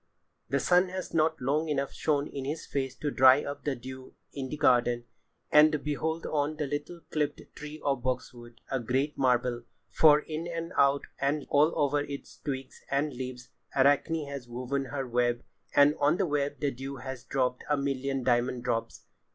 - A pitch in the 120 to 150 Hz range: Yes, medium, 140 Hz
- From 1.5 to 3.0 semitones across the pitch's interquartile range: Yes, narrow, 2.6 semitones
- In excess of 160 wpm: Yes, average, 185 wpm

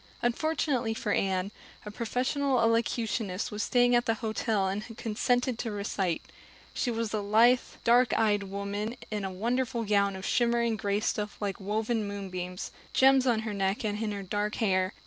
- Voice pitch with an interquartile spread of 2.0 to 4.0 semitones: Yes, average, 2.9 semitones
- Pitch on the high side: Yes, high, 215 Hz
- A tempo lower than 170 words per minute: No, average, 175 wpm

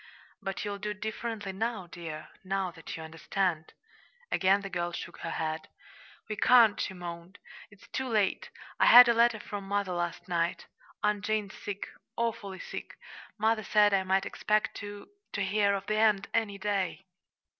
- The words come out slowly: No, average, 165 wpm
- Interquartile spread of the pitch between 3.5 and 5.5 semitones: No, narrow, 2.6 semitones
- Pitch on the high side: Yes, high, 200 Hz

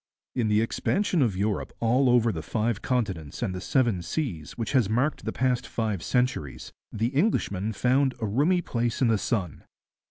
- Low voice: Yes, low, 115 Hz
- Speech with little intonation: No, average, 3.9 semitones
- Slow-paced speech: No, average, 180 wpm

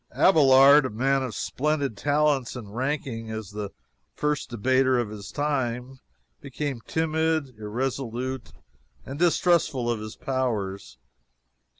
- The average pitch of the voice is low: Yes, low, 130 Hz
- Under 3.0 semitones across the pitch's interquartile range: No, average, 3.9 semitones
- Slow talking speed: Yes, slow, 115 wpm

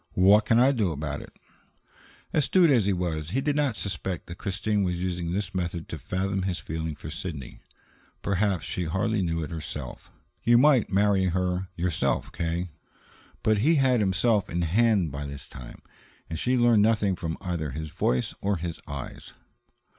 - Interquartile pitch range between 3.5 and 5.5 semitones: Yes, average, 4.2 semitones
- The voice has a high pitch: No, very low, 95 Hz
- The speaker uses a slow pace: No, average, 175 wpm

